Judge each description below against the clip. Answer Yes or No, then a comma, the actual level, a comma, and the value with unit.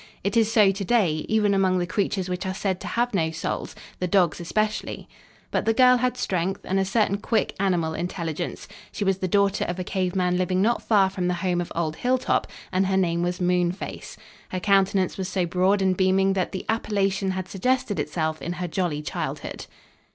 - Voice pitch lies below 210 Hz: Yes, high, 190 Hz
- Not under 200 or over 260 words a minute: Yes, fast, 205 wpm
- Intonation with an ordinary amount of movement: No, narrow, 2.0 semitones